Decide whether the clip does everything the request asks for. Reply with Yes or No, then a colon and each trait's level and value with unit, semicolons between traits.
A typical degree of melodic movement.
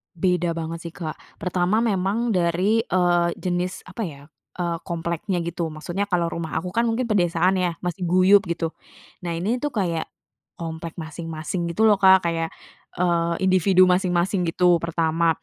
No: narrow, 2.1 semitones